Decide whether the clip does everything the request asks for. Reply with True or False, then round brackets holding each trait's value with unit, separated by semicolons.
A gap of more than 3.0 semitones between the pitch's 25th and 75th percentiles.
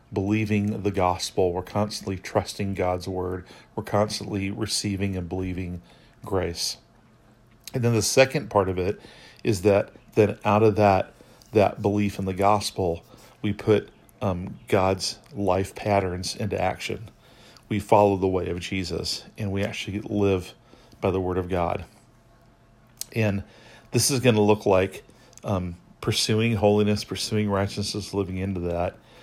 False (2.7 semitones)